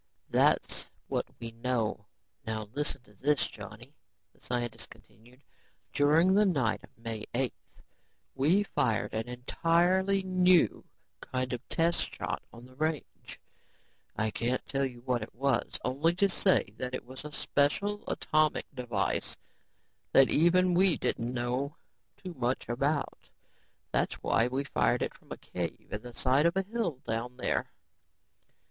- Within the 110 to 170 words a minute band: Yes, average, 150 wpm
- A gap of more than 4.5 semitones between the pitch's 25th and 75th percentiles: Yes, wide, 5.6 semitones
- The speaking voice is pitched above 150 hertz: No, low, 135 Hz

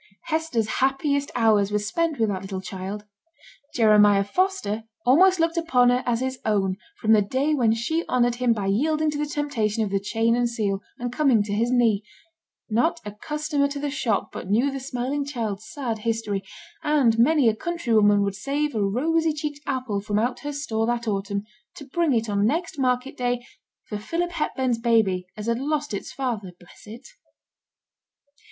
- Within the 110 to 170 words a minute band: No, average, 185 wpm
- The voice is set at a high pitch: Yes, high, 240 Hz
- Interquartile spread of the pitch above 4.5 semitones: Yes, wide, 5.4 semitones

